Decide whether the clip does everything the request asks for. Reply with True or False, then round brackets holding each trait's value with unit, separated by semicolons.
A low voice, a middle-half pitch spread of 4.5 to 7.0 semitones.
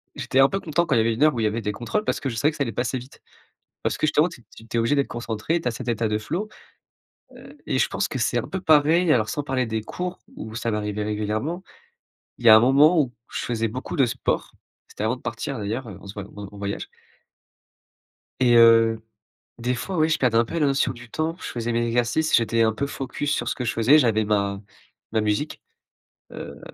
True (120 Hz; 4.8 semitones)